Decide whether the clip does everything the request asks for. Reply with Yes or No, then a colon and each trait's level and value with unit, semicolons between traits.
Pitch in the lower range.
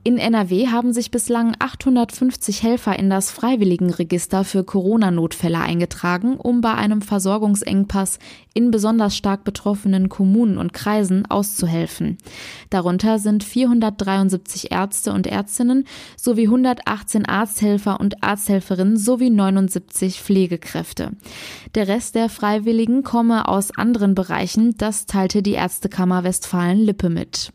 No: high, 205 Hz